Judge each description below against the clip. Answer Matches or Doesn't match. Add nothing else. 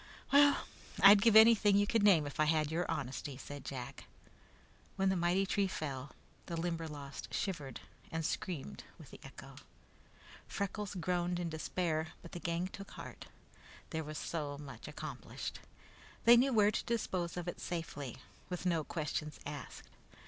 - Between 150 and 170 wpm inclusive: Matches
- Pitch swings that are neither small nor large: Matches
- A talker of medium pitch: Matches